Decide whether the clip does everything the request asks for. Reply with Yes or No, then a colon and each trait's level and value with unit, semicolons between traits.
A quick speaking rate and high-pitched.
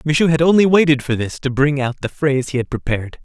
No: fast, 260 wpm; medium, 140 Hz